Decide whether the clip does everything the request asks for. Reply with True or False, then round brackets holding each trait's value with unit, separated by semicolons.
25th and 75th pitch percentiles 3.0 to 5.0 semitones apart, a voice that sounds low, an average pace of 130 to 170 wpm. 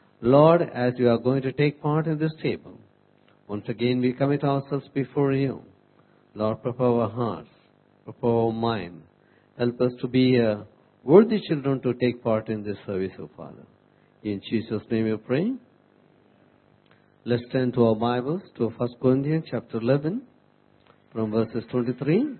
True (3.6 semitones; 125 Hz; 160 wpm)